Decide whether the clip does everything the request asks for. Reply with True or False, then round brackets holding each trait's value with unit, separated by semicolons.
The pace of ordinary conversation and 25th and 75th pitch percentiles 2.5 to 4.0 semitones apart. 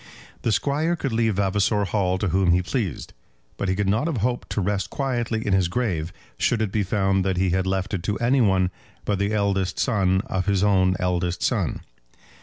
False (210 wpm; 3.0 semitones)